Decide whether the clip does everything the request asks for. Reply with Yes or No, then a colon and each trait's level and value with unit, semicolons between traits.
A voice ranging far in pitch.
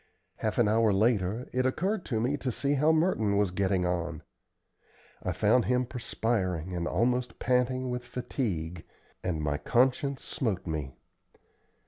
Yes: wide, 5.7 semitones